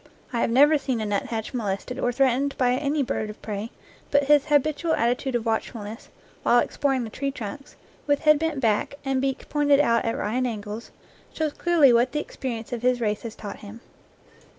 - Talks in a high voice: Yes, very high, 250 Hz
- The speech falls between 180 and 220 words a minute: Yes, average, 195 wpm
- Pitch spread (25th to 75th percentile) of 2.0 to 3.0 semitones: No, average, 3.9 semitones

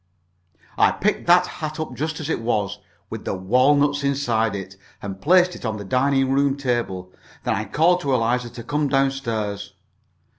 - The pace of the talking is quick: No, average, 180 wpm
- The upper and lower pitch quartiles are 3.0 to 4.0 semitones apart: No, average, 5.0 semitones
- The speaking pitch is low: Yes, low, 130 Hz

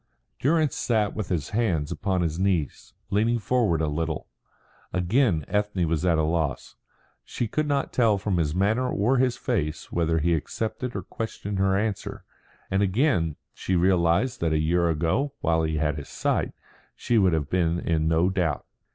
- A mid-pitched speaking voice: No, very low, 90 Hz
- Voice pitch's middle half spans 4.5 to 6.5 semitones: Yes, average, 5.1 semitones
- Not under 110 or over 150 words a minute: No, average, 175 wpm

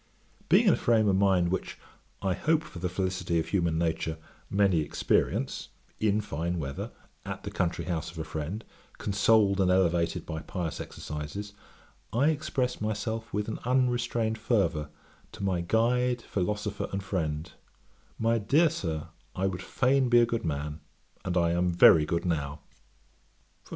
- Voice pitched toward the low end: Yes, very low, 95 Hz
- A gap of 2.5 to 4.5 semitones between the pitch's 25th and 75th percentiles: No, average, 5.0 semitones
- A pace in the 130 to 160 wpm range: Yes, average, 155 wpm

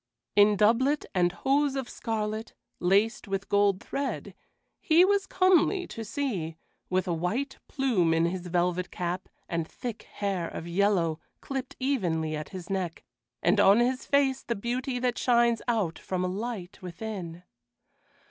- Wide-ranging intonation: Yes, wide, 6.1 semitones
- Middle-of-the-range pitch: No, high, 205 Hz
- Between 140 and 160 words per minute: Yes, average, 150 wpm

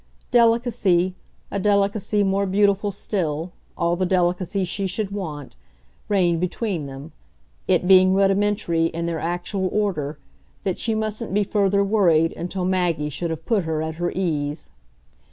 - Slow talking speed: No, average, 145 wpm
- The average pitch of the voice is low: No, medium, 185 Hz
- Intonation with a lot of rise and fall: No, average, 3.1 semitones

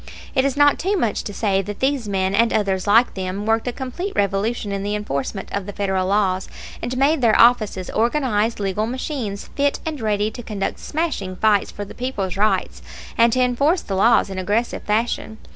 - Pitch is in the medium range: No, high, 215 Hz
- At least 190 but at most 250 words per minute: Yes, average, 195 wpm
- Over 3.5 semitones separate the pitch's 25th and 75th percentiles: Yes, average, 4.0 semitones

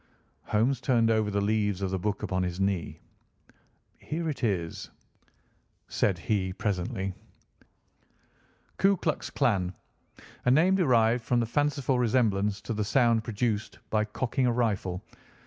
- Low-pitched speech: Yes, low, 110 Hz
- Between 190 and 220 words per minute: No, slow, 135 wpm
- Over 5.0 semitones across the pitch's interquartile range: No, average, 3.9 semitones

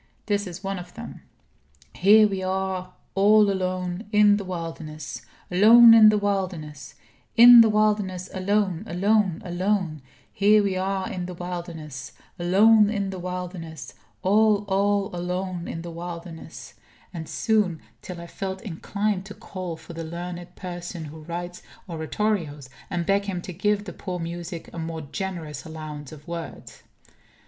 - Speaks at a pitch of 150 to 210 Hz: Yes, medium, 185 Hz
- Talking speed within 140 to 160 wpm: Yes, average, 150 wpm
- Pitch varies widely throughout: No, average, 3.0 semitones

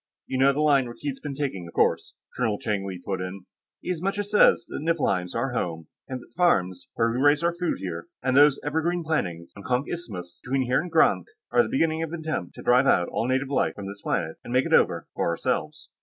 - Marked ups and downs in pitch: Yes, wide, 7.9 semitones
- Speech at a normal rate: No, fast, 240 wpm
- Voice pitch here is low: Yes, low, 130 Hz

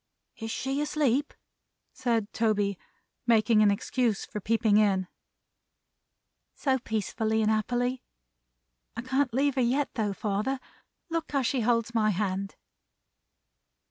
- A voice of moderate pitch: No, high, 230 Hz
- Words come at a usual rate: No, slow, 120 wpm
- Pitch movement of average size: Yes, average, 3.5 semitones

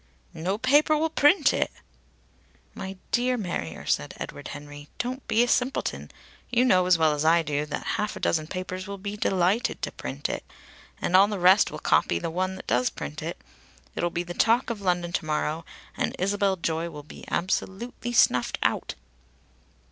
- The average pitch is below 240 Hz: Yes, medium, 185 Hz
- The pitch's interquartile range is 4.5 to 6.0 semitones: Yes, average, 5.2 semitones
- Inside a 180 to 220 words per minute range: Yes, average, 185 wpm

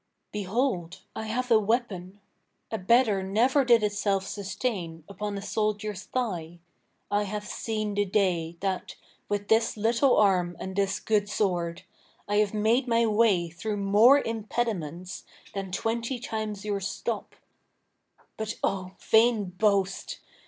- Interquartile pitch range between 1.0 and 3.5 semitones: Yes, average, 2.7 semitones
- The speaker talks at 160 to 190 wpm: No, slow, 135 wpm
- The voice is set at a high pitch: Yes, high, 205 Hz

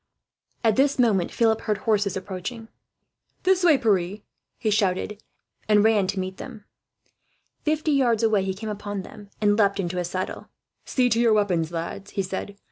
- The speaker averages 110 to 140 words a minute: No, average, 170 wpm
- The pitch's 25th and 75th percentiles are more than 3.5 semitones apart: No, average, 3.0 semitones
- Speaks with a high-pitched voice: Yes, high, 205 Hz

